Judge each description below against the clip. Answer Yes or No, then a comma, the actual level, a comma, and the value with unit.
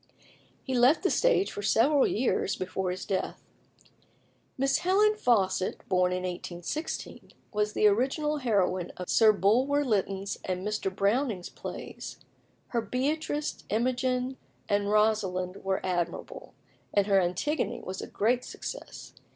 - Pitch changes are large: Yes, wide, 5.7 semitones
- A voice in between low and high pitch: No, high, 210 Hz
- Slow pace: Yes, slow, 130 wpm